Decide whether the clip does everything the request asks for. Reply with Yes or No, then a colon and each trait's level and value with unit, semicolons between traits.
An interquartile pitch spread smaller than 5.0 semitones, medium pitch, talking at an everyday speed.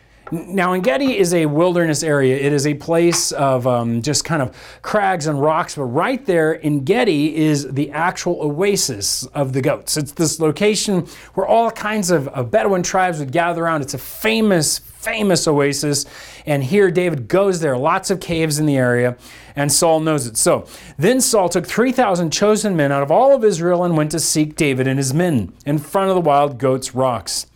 Yes: average, 4.4 semitones; medium, 160 Hz; average, 195 wpm